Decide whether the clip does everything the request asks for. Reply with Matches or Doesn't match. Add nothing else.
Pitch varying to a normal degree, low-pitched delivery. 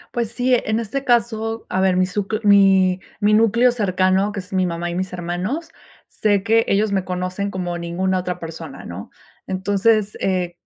Doesn't match